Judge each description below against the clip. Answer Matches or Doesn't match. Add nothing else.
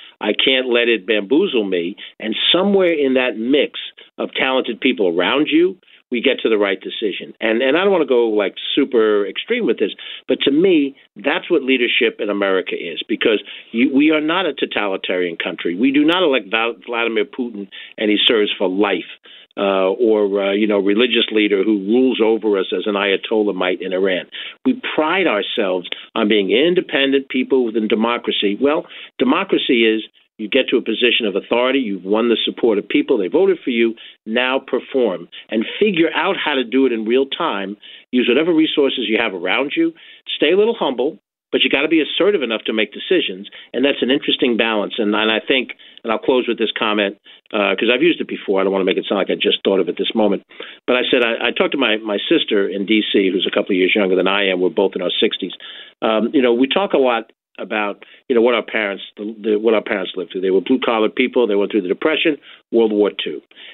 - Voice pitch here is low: Matches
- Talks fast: Matches